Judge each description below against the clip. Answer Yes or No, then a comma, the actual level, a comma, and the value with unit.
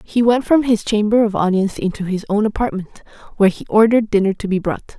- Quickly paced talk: Yes, fast, 215 wpm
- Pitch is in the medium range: No, high, 210 Hz